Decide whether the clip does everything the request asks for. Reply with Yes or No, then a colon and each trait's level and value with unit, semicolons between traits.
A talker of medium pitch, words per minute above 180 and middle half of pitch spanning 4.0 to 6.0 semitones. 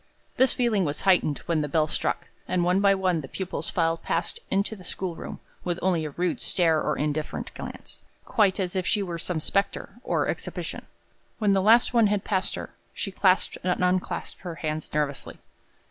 No: medium, 180 Hz; average, 190 wpm; average, 3.2 semitones